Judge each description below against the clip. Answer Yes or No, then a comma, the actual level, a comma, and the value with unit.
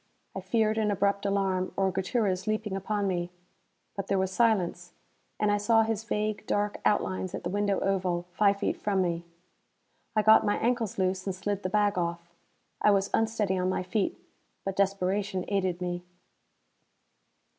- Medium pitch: No, high, 195 Hz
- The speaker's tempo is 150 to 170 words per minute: Yes, average, 165 wpm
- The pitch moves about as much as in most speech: No, narrow, 2.1 semitones